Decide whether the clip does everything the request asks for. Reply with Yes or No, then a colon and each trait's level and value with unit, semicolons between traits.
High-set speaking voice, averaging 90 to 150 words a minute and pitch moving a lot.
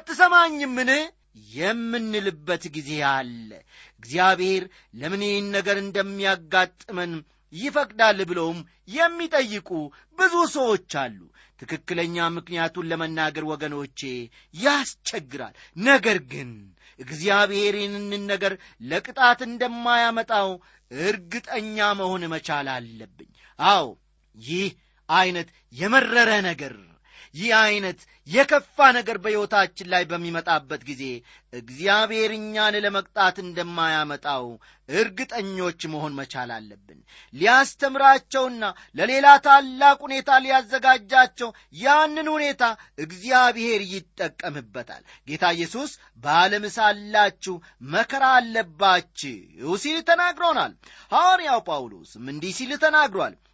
No: high, 200 Hz; average, 80 wpm; wide, 7.6 semitones